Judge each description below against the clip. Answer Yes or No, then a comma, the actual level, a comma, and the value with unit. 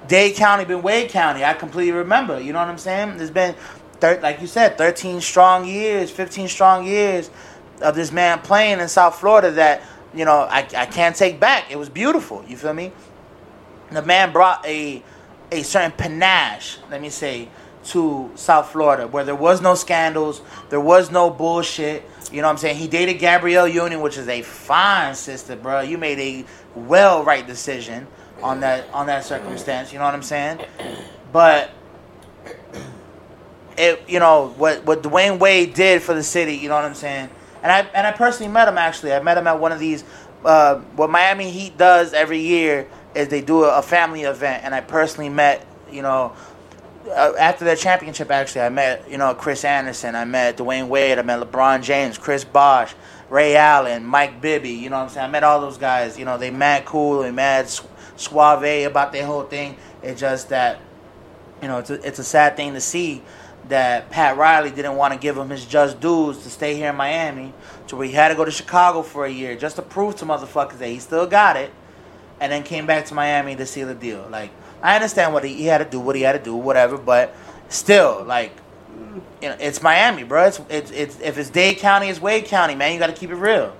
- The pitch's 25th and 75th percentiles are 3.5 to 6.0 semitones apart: Yes, average, 3.9 semitones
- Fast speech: Yes, fast, 215 wpm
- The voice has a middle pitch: Yes, medium, 150 Hz